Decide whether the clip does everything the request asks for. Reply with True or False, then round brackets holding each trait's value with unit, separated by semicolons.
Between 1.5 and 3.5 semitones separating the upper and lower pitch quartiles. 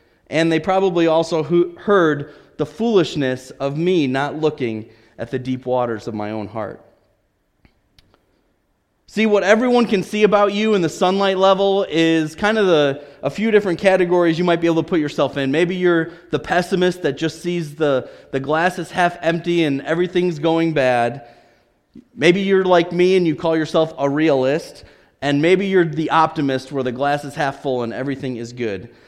False (4.6 semitones)